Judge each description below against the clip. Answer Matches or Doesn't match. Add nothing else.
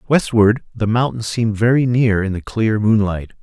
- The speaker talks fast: Doesn't match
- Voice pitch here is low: Matches